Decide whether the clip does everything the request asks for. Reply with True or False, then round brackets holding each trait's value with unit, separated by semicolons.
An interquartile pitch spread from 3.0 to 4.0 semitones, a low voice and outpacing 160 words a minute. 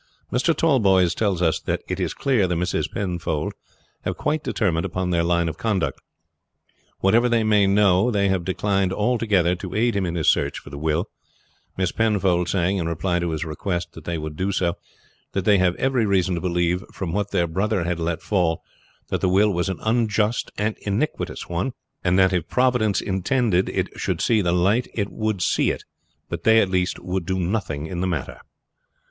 True (3.4 semitones; 95 Hz; 195 wpm)